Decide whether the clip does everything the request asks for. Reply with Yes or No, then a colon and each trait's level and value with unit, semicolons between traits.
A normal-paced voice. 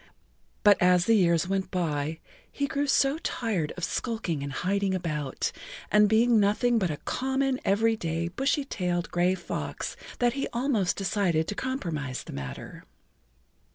Yes: average, 155 wpm